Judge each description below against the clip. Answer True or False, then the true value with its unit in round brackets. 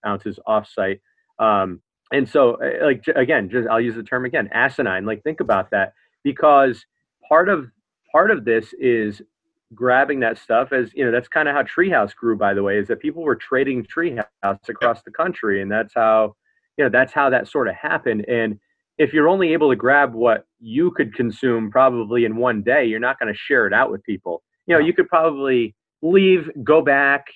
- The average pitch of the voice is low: True (125 Hz)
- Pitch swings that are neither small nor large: False (6.5 semitones)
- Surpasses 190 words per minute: True (205 wpm)